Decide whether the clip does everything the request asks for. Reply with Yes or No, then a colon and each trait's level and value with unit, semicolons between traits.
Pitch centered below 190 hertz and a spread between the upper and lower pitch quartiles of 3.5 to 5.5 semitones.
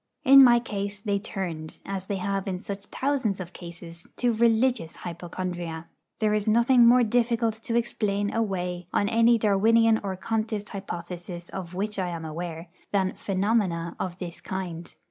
No: high, 200 Hz; average, 4.2 semitones